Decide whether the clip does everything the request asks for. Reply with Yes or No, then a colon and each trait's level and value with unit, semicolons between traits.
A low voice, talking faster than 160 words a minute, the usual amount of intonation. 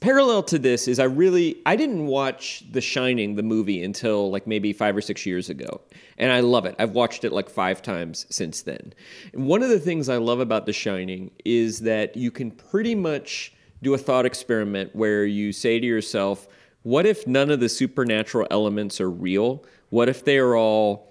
Yes: low, 115 Hz; average, 200 wpm; average, 4.0 semitones